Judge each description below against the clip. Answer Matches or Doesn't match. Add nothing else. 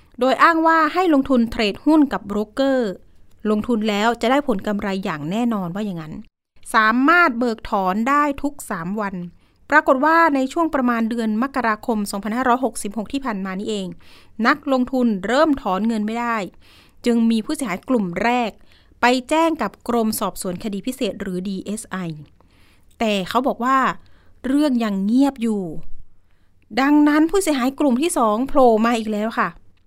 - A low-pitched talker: Doesn't match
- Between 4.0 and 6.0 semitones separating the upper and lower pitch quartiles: Matches